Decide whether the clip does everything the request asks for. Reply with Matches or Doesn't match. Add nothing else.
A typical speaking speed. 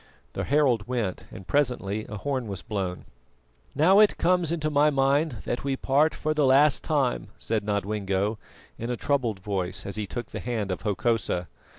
Matches